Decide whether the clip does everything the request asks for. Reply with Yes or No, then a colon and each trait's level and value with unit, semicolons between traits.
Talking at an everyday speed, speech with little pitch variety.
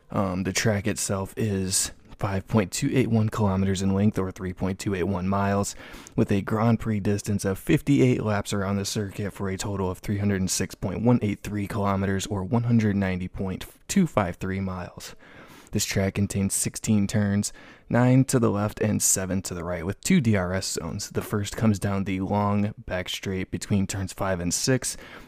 Yes: average, 150 wpm; narrow, 2.2 semitones